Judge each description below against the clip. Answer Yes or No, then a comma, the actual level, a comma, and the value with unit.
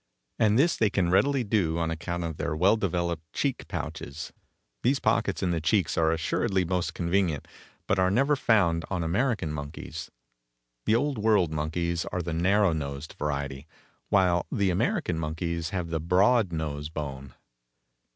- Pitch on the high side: No, very low, 85 Hz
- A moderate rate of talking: Yes, average, 160 wpm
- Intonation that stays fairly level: No, average, 4.0 semitones